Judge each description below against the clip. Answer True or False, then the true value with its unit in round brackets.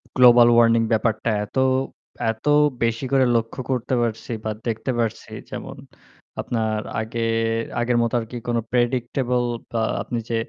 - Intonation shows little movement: True (1.4 semitones)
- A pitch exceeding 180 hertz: False (115 Hz)